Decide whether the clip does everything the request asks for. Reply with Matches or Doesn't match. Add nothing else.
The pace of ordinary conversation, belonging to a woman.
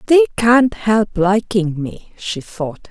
Matches